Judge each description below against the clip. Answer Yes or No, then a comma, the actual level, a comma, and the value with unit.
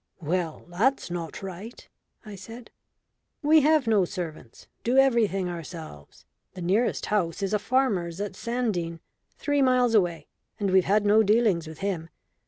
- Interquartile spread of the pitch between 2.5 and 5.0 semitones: No, wide, 5.4 semitones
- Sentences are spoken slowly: No, average, 150 wpm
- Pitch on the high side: Yes, high, 200 Hz